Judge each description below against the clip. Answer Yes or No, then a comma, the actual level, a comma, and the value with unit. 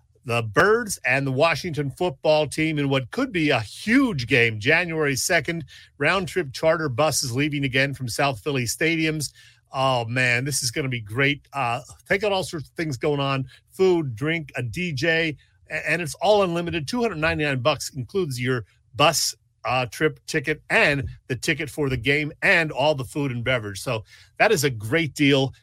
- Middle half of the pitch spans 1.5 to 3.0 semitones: No, average, 4.1 semitones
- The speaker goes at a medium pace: Yes, average, 180 wpm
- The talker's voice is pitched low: No, medium, 145 Hz